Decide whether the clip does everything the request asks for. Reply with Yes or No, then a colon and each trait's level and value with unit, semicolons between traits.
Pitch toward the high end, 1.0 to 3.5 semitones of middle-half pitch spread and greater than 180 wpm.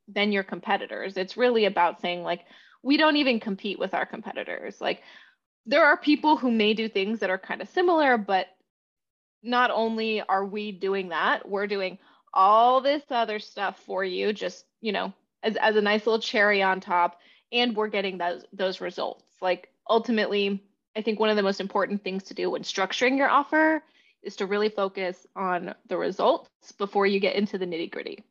No: high, 205 Hz; average, 3.9 semitones; average, 190 wpm